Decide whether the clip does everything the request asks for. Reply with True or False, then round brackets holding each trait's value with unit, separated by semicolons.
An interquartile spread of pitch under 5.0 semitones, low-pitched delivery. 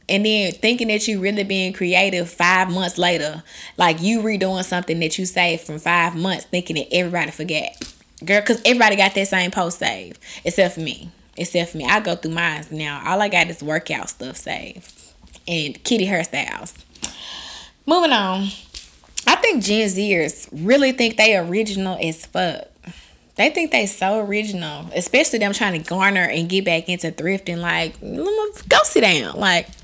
False (3.4 semitones; 185 Hz)